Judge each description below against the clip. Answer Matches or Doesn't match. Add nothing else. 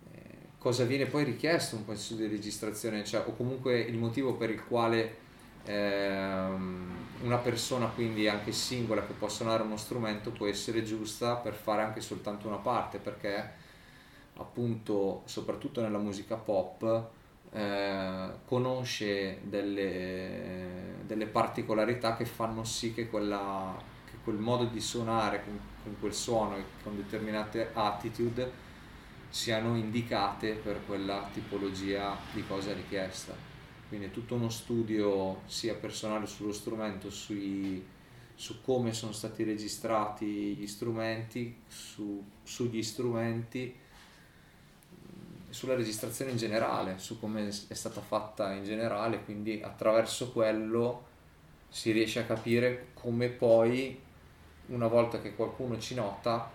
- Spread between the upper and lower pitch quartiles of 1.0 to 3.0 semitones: Matches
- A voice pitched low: Matches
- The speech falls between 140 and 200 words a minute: Doesn't match